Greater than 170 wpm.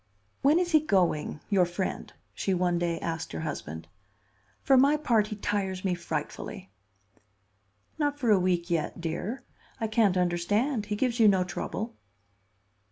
No: average, 150 wpm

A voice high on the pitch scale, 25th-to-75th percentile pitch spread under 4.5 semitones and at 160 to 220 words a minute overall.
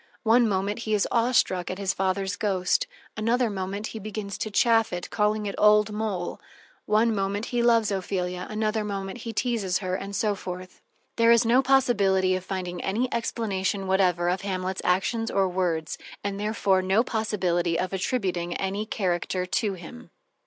Yes: high, 200 Hz; average, 2.8 semitones; average, 170 wpm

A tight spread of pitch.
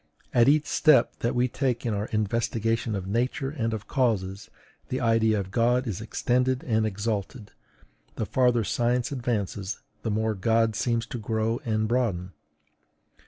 Yes: narrow, 2.3 semitones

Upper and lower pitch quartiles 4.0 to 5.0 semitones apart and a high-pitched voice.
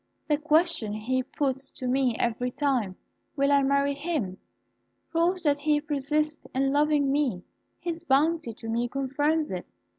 No: average, 3.1 semitones; very high, 280 Hz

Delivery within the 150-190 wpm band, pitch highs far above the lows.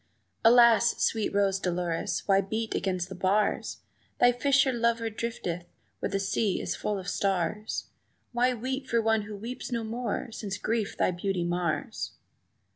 No: average, 155 wpm; average, 3.4 semitones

